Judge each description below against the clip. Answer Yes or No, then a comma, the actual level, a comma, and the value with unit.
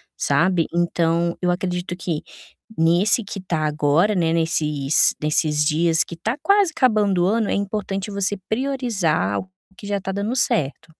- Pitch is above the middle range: No, medium, 180 Hz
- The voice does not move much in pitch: No, average, 4.0 semitones